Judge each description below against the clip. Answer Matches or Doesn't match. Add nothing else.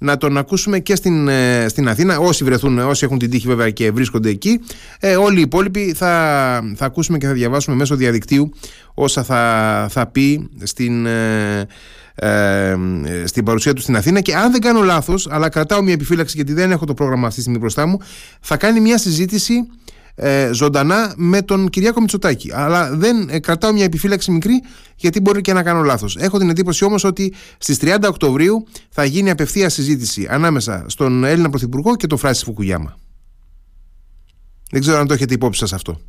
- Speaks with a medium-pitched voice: Matches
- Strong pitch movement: Matches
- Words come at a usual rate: Doesn't match